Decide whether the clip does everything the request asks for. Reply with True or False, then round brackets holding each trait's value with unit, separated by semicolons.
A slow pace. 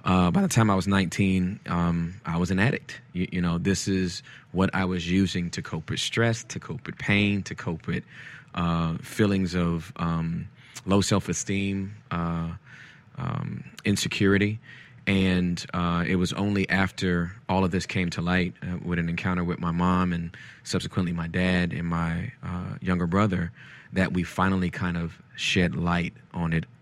False (175 wpm)